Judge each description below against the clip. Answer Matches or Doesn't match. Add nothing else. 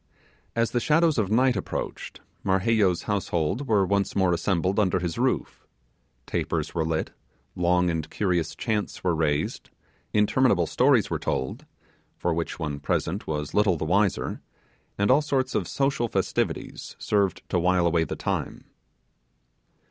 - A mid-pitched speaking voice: Doesn't match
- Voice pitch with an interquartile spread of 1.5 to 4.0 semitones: Doesn't match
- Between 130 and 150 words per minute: Matches